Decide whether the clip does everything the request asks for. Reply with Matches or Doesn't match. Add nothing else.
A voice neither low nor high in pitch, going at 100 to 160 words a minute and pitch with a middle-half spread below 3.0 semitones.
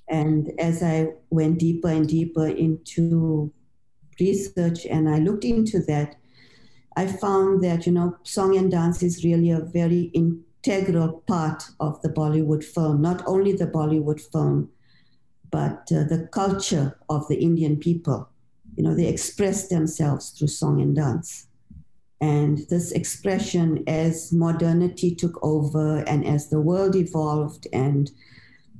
Matches